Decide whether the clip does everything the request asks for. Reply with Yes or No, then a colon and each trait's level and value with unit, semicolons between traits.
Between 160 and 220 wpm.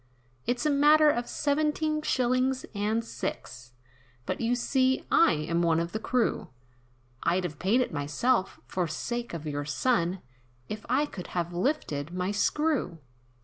No: average, 150 wpm